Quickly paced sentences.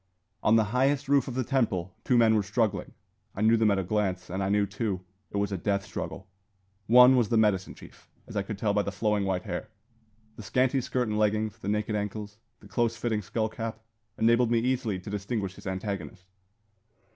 Yes: fast, 210 wpm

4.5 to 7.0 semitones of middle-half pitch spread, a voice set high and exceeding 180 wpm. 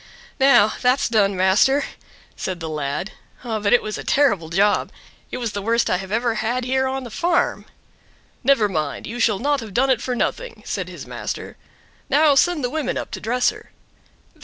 Yes: average, 4.8 semitones; high, 235 Hz; average, 190 wpm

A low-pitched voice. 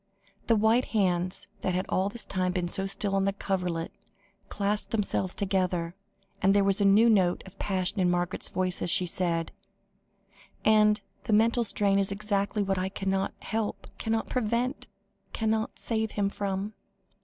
No: high, 195 Hz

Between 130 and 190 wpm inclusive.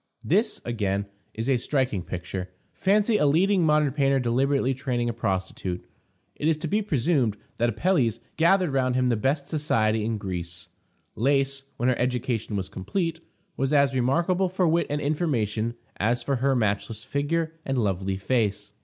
Yes: average, 165 wpm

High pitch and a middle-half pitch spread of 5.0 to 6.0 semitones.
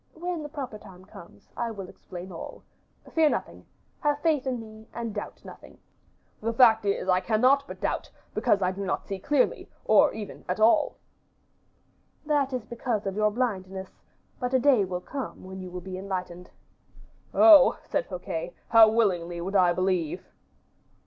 Yes: high, 215 Hz; wide, 5.6 semitones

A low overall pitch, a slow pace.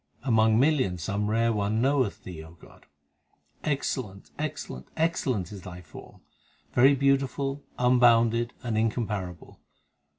Yes: low, 115 Hz; slow, 110 wpm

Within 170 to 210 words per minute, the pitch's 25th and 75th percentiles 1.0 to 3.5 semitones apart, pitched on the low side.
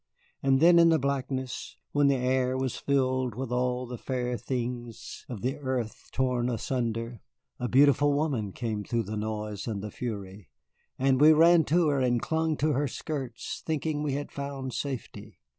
Yes: average, 175 wpm; average, 3.2 semitones; low, 130 Hz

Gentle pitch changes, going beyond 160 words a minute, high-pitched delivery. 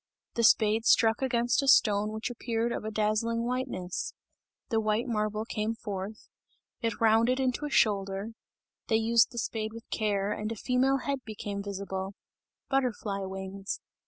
No: narrow, 2.3 semitones; average, 155 wpm; high, 220 Hz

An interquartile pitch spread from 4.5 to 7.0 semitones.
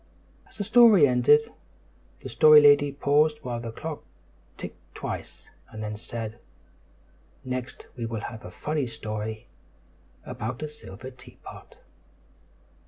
Yes: average, 5.1 semitones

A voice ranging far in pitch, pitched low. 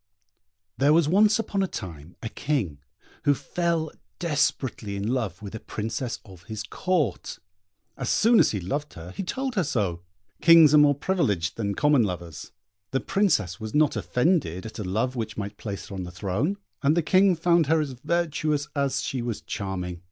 Yes: wide, 8.3 semitones; low, 130 Hz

